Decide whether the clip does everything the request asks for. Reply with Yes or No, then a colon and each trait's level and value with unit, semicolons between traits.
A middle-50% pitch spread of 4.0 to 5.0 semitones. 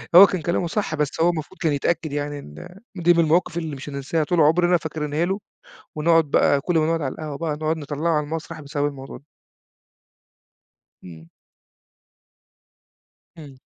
No: narrow, 2.6 semitones